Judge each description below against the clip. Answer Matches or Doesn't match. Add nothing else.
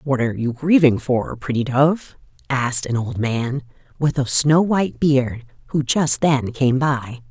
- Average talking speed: Matches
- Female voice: Matches